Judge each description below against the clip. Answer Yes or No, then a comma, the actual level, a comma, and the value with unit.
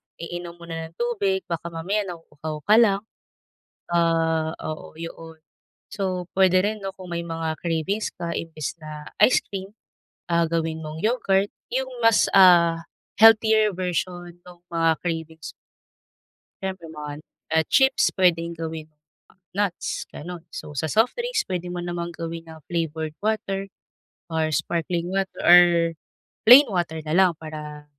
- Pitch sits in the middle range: Yes, medium, 170 Hz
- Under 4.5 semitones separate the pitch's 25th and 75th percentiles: Yes, average, 2.9 semitones